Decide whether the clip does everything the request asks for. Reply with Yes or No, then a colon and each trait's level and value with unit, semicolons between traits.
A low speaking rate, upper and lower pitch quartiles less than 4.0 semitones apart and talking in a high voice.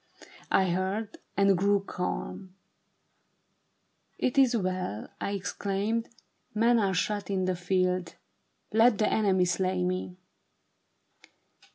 Yes: slow, 115 wpm; narrow, 2.5 semitones; high, 195 Hz